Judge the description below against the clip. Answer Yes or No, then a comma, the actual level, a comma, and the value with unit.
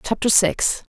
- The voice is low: No, high, 205 Hz